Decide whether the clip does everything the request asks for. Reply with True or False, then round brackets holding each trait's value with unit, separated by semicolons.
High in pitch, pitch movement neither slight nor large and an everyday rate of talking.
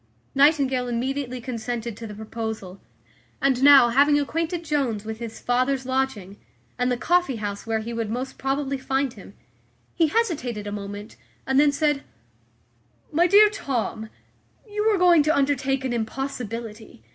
True (260 Hz; 4.1 semitones; 150 wpm)